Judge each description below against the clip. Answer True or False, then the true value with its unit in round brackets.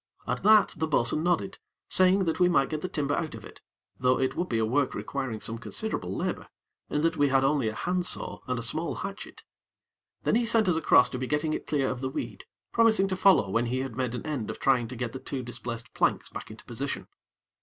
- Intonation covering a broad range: True (6.0 semitones)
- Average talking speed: False (240 wpm)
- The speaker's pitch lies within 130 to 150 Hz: True (140 Hz)